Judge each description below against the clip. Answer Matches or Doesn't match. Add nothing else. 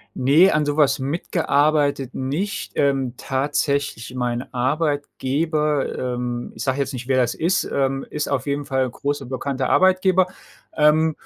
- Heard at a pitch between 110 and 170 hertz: Matches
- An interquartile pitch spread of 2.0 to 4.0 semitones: Matches